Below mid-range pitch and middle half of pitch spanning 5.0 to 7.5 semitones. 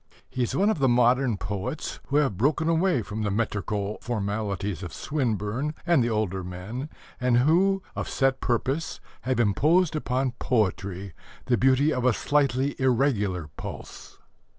Yes: low, 125 Hz; wide, 5.5 semitones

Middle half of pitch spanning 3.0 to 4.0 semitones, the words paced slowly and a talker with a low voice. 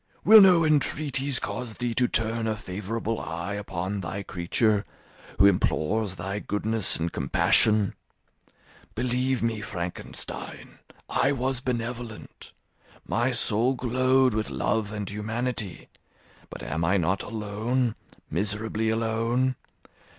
Yes: average, 3.5 semitones; slow, 115 wpm; low, 110 Hz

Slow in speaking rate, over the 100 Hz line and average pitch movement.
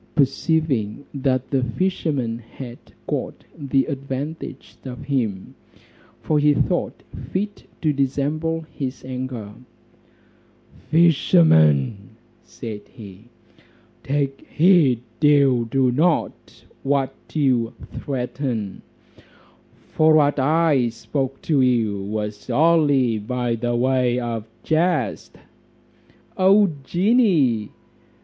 Yes: slow, 90 wpm; low, 135 Hz; average, 4.5 semitones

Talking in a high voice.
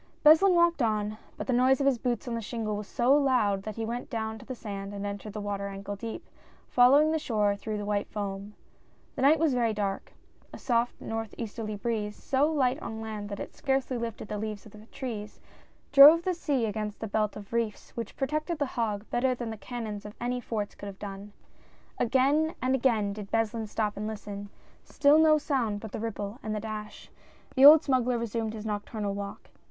Yes: high, 225 Hz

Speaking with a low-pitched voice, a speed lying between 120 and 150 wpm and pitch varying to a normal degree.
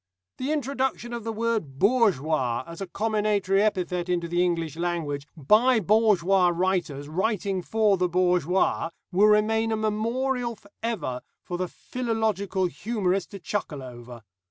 No: high, 195 Hz; average, 140 wpm; average, 4.4 semitones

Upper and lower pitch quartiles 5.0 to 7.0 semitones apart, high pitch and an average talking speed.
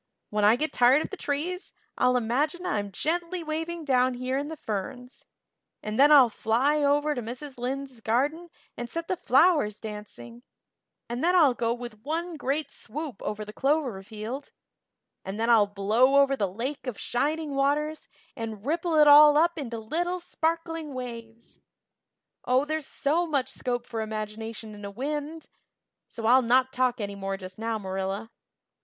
Yes: average, 5.3 semitones; very high, 255 Hz; average, 170 wpm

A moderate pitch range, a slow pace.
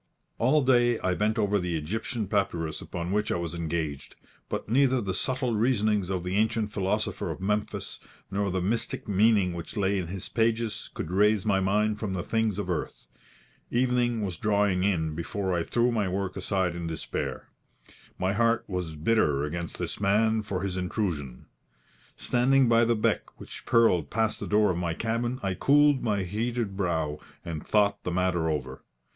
No: average, 4.0 semitones; average, 175 wpm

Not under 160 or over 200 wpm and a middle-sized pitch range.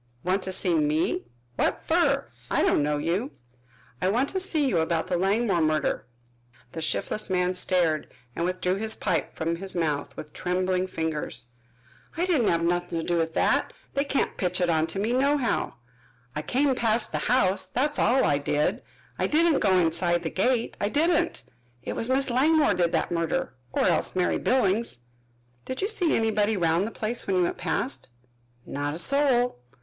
No: average, 180 wpm; wide, 6.7 semitones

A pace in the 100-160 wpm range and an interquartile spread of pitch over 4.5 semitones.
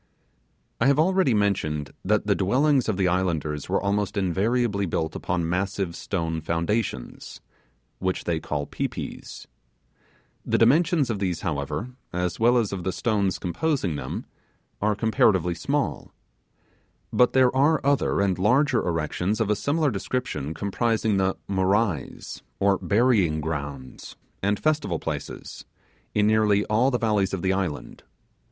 Yes: average, 140 wpm; average, 4.9 semitones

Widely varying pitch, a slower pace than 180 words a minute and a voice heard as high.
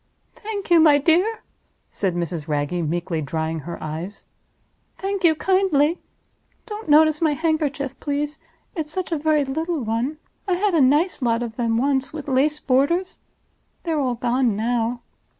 Yes: wide, 6.0 semitones; average, 155 wpm; very high, 285 Hz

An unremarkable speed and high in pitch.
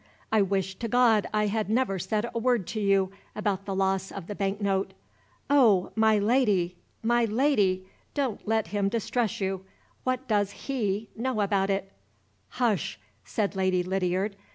Yes: average, 160 wpm; high, 205 Hz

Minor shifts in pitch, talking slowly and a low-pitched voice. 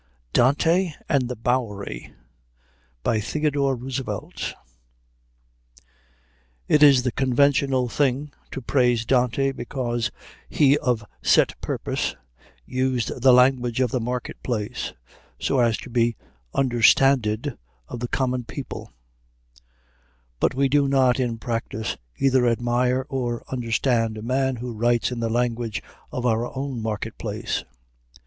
Yes: narrow, 2.3 semitones; slow, 120 wpm; low, 125 Hz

